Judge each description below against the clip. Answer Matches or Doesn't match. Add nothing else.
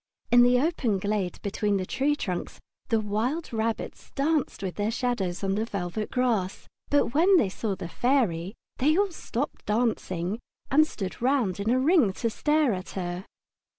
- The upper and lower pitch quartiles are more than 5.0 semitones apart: Matches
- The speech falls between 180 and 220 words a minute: Doesn't match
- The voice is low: Doesn't match